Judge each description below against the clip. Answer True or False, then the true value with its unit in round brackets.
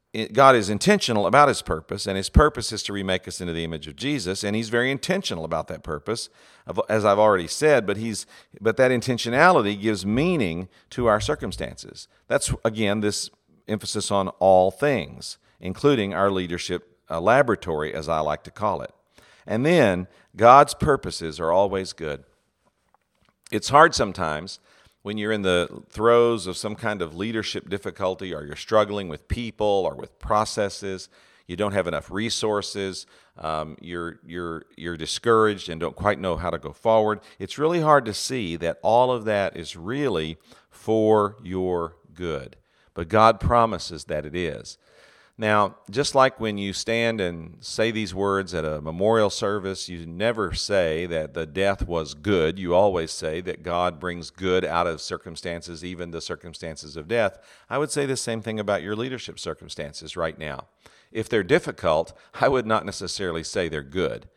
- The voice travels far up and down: False (4.2 semitones)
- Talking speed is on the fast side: False (170 wpm)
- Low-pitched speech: True (100 Hz)